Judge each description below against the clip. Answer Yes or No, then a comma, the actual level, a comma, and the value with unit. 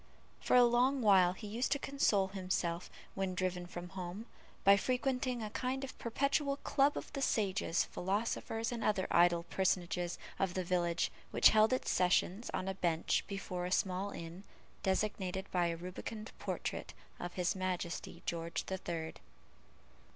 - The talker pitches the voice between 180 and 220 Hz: Yes, high, 190 Hz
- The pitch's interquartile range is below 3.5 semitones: No, average, 4.2 semitones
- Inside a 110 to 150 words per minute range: No, average, 160 wpm